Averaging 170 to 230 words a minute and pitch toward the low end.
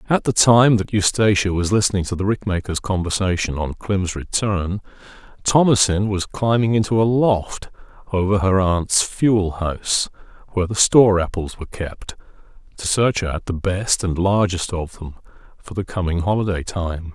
No: average, 155 wpm; very low, 95 Hz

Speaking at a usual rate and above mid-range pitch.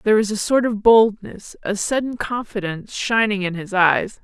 Yes: average, 185 wpm; high, 210 Hz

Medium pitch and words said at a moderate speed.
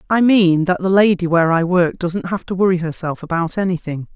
No: medium, 175 Hz; fast, 215 wpm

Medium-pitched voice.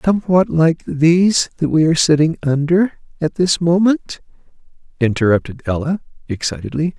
Yes: medium, 155 Hz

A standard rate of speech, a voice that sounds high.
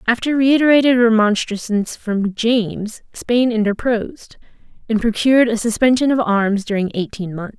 No: slow, 125 wpm; high, 225 Hz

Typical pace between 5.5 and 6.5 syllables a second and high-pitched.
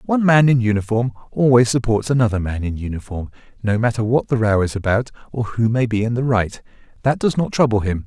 No: 6.0 syllables/s; low, 115 Hz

